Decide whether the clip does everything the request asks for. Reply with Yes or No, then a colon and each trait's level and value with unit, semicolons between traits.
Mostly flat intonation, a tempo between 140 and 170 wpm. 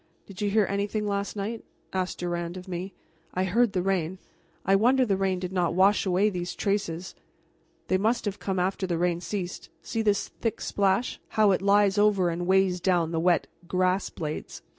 No: narrow, 2.3 semitones; average, 190 wpm